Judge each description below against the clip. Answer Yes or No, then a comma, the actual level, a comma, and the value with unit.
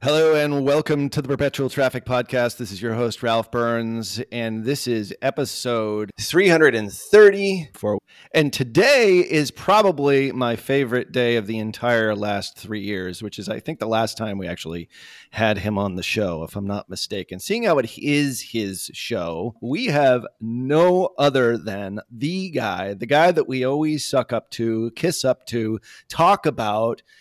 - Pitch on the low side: Yes, low, 120 Hz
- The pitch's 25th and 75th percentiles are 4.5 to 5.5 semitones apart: Yes, average, 4.8 semitones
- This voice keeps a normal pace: Yes, average, 170 wpm